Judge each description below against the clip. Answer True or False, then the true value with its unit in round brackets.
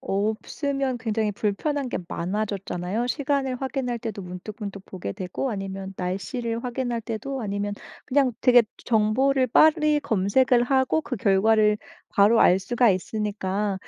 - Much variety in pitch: False (4.6 semitones)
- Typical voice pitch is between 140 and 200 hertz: False (220 Hz)